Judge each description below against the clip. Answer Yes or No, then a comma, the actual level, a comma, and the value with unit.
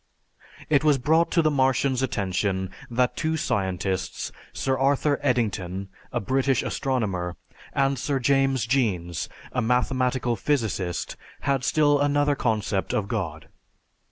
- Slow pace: Yes, slow, 125 wpm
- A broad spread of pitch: Yes, wide, 5.8 semitones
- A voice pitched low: Yes, low, 125 Hz